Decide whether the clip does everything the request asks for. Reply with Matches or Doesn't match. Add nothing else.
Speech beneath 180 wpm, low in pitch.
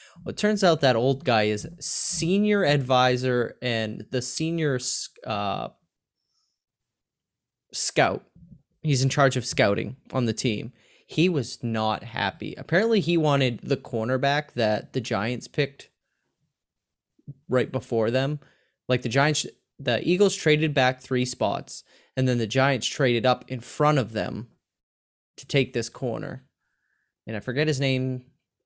Matches